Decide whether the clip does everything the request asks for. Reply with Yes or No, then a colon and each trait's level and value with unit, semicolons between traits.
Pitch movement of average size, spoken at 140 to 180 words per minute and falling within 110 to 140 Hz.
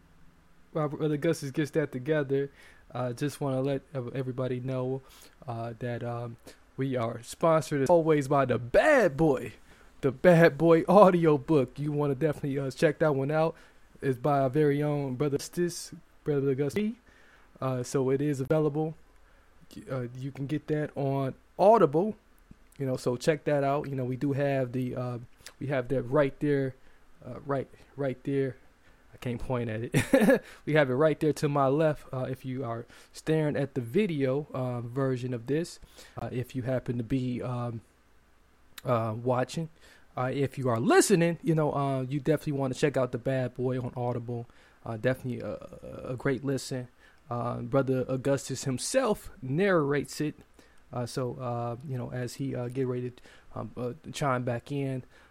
Yes: average, 3.1 semitones; average, 175 wpm; low, 135 Hz